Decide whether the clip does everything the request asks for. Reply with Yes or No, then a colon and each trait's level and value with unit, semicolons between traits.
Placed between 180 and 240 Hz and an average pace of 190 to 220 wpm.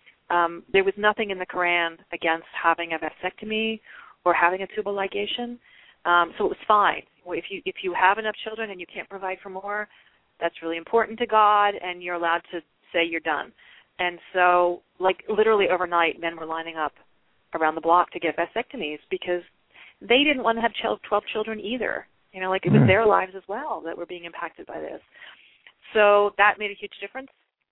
Yes: medium, 185 Hz; average, 195 wpm